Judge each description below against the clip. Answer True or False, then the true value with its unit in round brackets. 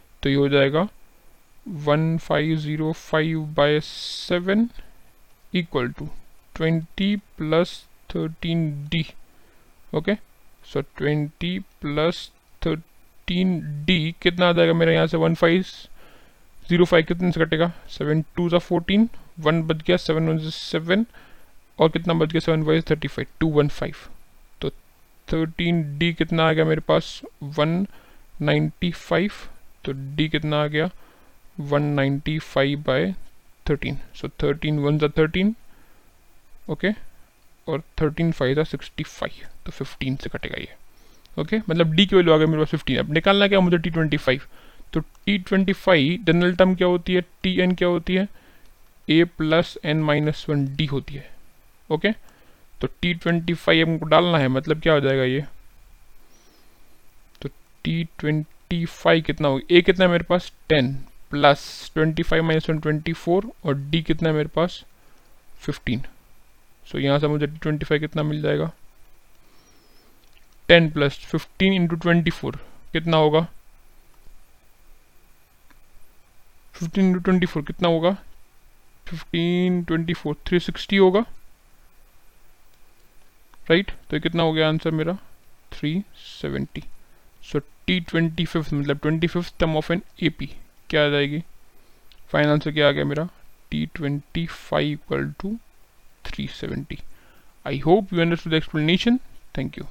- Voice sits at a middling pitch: True (160 Hz)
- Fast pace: False (140 wpm)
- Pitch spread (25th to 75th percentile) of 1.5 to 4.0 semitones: True (2.9 semitones)